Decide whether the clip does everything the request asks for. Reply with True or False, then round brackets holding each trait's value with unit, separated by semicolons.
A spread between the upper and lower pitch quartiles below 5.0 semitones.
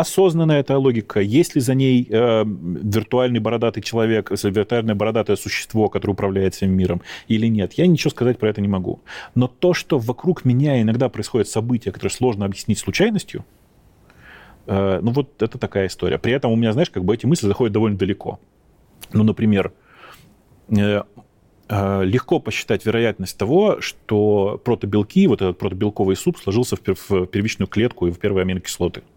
True (3.9 semitones)